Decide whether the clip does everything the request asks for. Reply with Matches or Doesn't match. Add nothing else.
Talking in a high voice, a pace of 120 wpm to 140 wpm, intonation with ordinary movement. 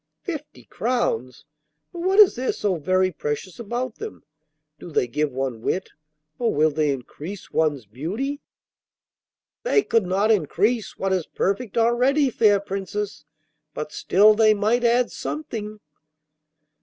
Doesn't match